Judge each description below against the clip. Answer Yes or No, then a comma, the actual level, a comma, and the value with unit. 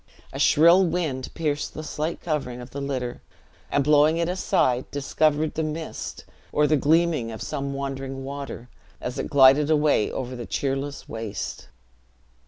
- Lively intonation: No, average, 2.8 semitones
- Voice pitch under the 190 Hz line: Yes, medium, 140 Hz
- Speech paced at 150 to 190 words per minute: Yes, average, 155 wpm